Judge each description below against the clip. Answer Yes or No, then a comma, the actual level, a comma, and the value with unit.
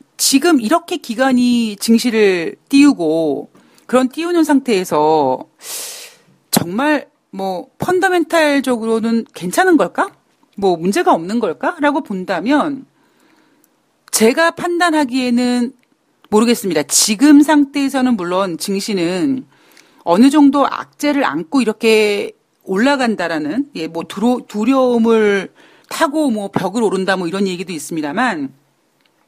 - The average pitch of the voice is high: Yes, very high, 255 Hz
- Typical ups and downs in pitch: No, wide, 6.9 semitones